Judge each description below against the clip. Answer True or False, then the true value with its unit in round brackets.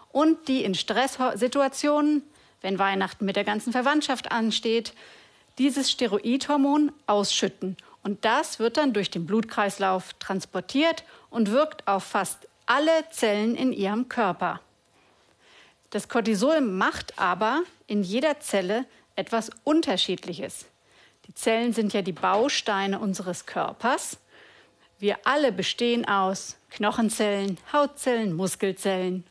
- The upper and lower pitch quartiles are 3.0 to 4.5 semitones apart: False (5.4 semitones)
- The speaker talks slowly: True (115 wpm)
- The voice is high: True (220 Hz)